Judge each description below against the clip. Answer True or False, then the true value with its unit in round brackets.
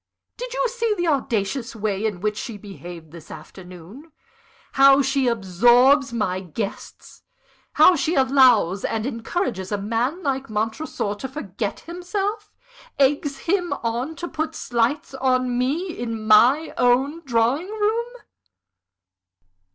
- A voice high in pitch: True (255 Hz)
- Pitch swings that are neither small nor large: False (6.5 semitones)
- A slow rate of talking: True (130 wpm)